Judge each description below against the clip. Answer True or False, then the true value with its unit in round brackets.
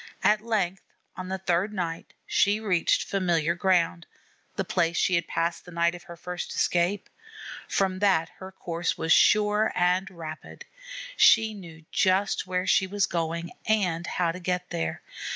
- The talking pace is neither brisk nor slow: True (160 wpm)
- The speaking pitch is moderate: True (180 Hz)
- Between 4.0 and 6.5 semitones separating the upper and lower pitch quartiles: False (2.4 semitones)